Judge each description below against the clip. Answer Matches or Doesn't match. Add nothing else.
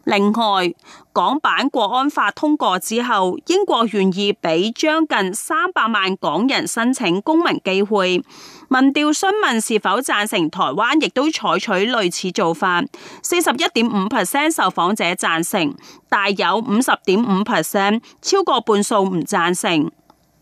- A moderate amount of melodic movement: Doesn't match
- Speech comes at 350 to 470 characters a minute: Doesn't match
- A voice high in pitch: Matches